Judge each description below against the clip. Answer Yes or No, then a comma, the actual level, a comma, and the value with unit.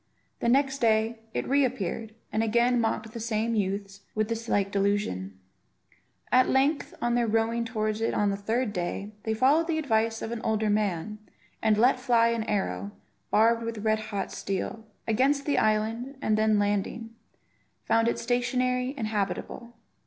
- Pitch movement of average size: No, narrow, 2.2 semitones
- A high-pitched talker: Yes, high, 225 Hz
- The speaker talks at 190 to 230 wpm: No, average, 165 wpm